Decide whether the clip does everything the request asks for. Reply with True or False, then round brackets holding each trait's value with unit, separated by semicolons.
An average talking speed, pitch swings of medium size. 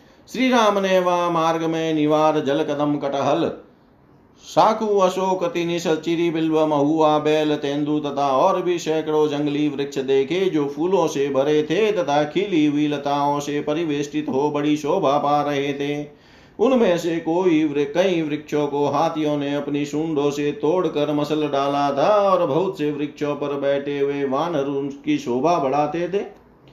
False (145 wpm; 2.3 semitones)